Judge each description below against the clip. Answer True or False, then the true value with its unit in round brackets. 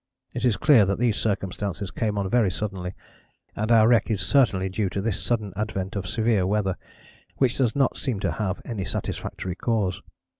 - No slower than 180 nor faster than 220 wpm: True (185 wpm)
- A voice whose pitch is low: True (105 Hz)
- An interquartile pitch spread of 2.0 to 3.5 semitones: True (3.2 semitones)